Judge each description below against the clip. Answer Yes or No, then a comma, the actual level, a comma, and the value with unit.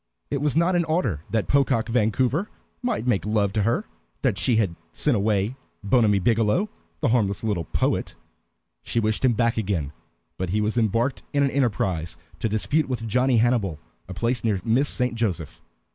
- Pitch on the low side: Yes, low, 115 Hz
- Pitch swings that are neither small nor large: Yes, average, 4.0 semitones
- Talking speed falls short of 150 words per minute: No, average, 180 wpm